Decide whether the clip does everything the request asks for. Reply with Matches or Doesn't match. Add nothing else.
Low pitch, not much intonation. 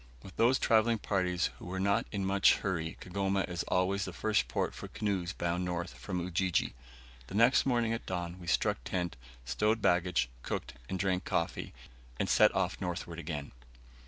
Matches